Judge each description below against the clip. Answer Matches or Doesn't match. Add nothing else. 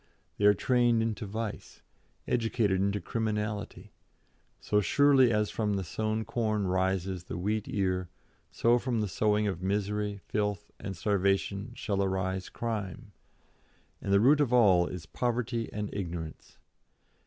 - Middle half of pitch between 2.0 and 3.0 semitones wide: Matches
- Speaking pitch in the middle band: Doesn't match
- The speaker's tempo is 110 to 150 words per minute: Matches